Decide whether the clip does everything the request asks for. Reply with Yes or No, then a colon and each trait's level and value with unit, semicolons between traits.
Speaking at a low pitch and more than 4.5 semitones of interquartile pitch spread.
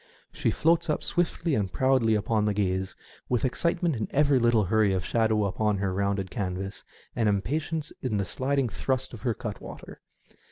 Yes: low, 110 Hz; average, 5.0 semitones